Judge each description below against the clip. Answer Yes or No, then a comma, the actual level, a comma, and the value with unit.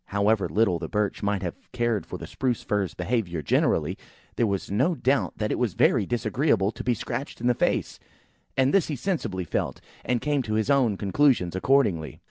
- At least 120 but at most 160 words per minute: No, average, 195 wpm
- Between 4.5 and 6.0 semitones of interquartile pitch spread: Yes, average, 5.0 semitones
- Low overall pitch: Yes, low, 110 Hz